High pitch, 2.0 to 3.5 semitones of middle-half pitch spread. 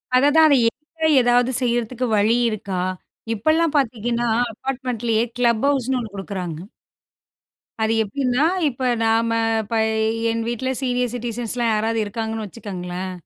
Yes: high, 235 Hz; average, 2.8 semitones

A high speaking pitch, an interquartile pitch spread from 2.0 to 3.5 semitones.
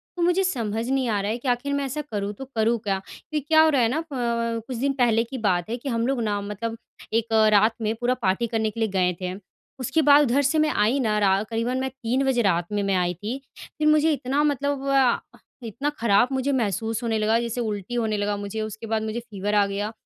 No: high, 230 Hz; average, 4.1 semitones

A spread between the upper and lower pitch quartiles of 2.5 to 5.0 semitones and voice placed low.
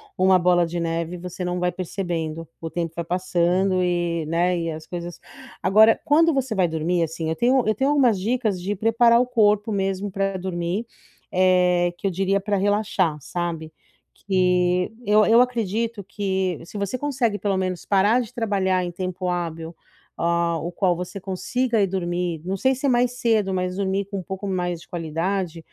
No: average, 3.0 semitones; medium, 185 Hz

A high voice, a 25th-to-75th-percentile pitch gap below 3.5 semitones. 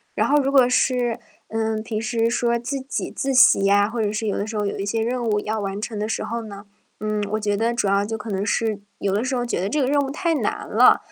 Yes: high, 225 Hz; average, 2.9 semitones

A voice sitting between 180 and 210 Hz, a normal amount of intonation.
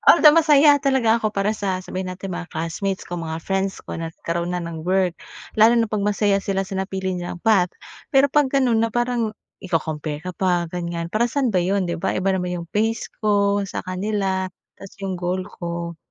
Yes: high, 190 Hz; average, 3.5 semitones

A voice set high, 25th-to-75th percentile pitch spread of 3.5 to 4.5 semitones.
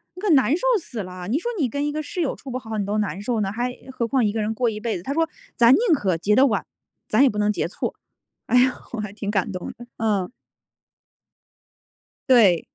Yes: high, 225 Hz; average, 4.0 semitones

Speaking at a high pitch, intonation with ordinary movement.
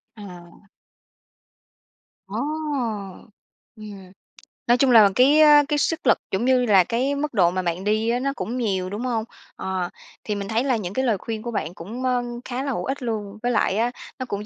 Yes: high, 225 Hz; average, 4.3 semitones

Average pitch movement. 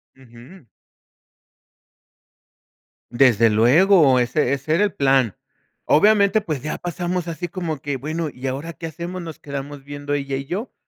Yes: average, 4.4 semitones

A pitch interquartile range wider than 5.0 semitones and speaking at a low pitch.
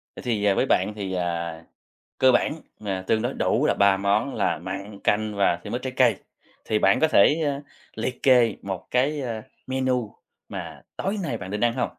No: average, 4.7 semitones; low, 110 Hz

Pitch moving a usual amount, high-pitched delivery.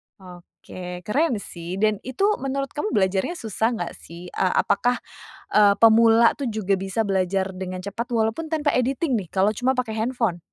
Yes: average, 4.7 semitones; high, 220 Hz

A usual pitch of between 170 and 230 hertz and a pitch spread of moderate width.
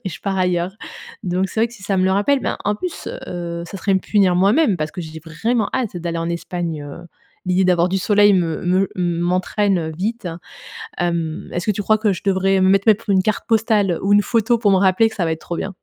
Yes: high, 190 Hz; average, 3.0 semitones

